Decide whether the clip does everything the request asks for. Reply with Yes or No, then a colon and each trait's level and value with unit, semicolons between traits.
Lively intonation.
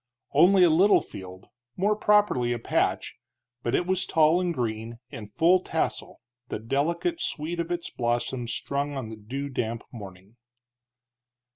Yes: wide, 7.1 semitones